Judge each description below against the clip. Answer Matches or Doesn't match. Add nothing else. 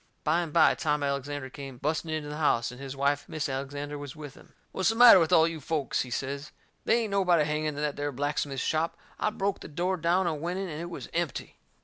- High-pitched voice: Doesn't match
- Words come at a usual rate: Doesn't match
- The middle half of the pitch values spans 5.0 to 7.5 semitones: Doesn't match